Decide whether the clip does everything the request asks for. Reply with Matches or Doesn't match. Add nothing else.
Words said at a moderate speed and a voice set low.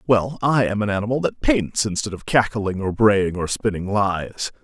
Matches